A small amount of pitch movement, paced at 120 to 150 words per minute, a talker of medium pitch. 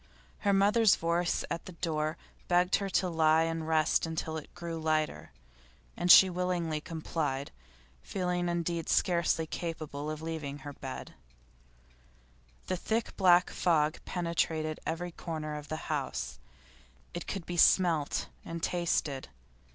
Yes: narrow, 2.1 semitones; slow, 135 wpm; medium, 165 Hz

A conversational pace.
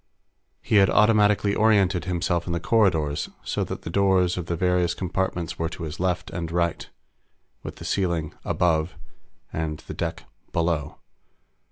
Yes: average, 155 wpm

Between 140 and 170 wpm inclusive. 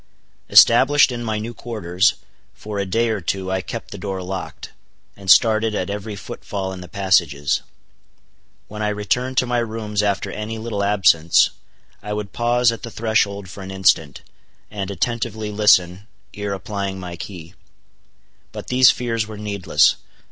Yes: average, 160 wpm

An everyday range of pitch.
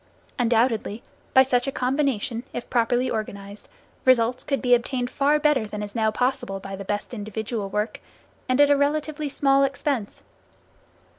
Yes: average, 4.1 semitones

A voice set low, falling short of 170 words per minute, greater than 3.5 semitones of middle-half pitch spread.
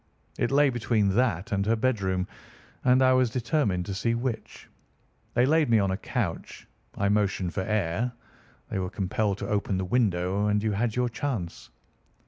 No: low, 105 Hz; average, 175 wpm; average, 4.1 semitones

